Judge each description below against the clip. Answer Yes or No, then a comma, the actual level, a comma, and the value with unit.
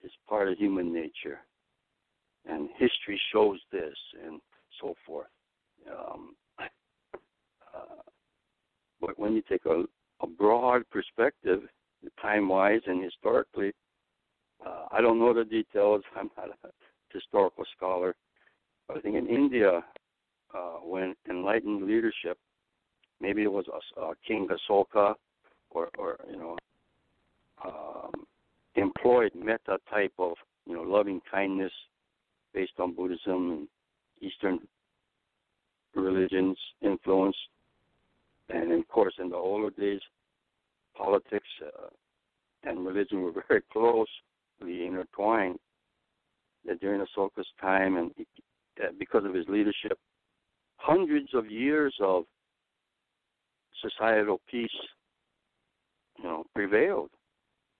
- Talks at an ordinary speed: No, slow, 110 wpm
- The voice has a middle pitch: No, low, 110 Hz